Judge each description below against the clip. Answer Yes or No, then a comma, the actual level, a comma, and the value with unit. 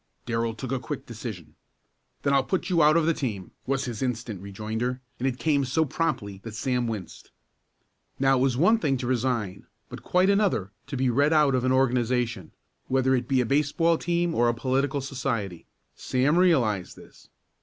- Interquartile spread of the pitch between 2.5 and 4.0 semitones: Yes, average, 3.7 semitones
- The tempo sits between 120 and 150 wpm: No, average, 185 wpm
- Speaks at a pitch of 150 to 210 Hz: No, low, 130 Hz